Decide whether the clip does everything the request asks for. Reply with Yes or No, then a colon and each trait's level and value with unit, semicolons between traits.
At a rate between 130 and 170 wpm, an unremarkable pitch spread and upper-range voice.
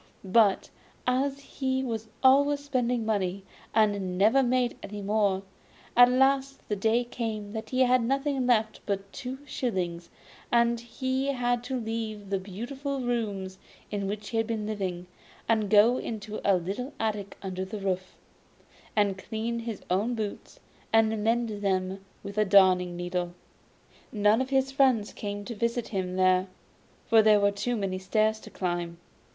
Yes: average, 155 wpm; average, 3.8 semitones; high, 220 Hz